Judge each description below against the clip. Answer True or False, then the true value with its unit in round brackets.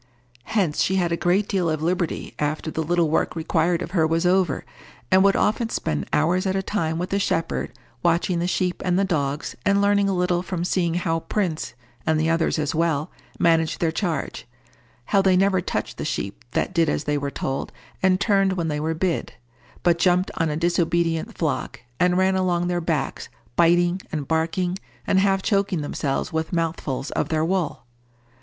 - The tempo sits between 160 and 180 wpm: False (190 wpm)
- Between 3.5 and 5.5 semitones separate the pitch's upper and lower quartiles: False (2.7 semitones)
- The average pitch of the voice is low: False (170 Hz)